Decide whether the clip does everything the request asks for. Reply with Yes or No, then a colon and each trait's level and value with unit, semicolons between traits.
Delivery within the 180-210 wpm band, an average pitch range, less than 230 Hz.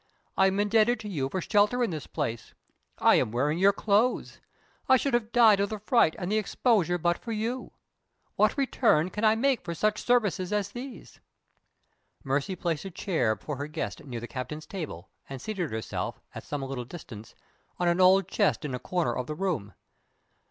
No: average, 195 wpm; wide, 6.6 semitones; medium, 185 Hz